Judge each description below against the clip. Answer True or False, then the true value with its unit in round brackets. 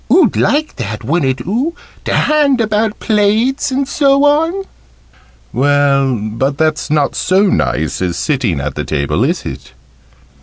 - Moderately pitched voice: True (170 Hz)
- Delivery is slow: False (145 wpm)